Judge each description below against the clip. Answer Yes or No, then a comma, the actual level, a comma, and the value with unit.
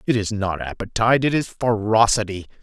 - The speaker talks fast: No, average, 160 wpm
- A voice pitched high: No, low, 110 Hz